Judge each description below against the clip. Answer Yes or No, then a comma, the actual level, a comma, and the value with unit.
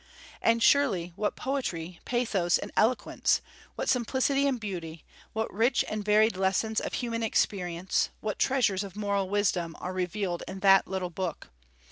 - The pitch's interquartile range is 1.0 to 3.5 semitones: No, average, 3.9 semitones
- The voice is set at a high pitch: Yes, high, 200 Hz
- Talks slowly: No, average, 150 wpm